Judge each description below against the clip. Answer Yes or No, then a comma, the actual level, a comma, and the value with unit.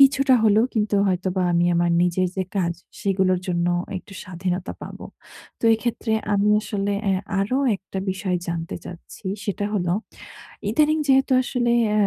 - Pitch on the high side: Yes, high, 195 Hz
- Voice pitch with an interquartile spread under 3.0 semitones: No, average, 3.4 semitones